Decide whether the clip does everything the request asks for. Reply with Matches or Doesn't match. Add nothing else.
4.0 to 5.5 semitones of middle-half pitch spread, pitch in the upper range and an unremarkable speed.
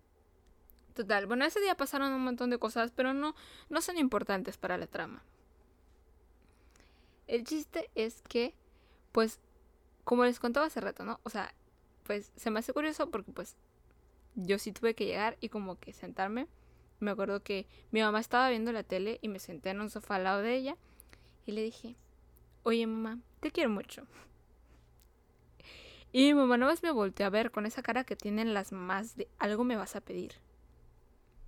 Matches